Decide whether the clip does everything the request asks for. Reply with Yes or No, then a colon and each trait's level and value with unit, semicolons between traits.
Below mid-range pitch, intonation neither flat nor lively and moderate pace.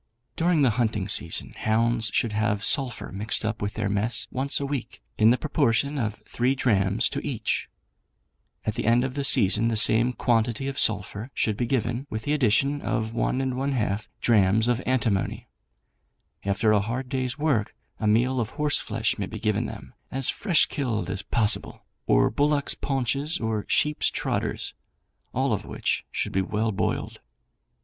Yes: low, 115 Hz; average, 3.7 semitones; average, 170 wpm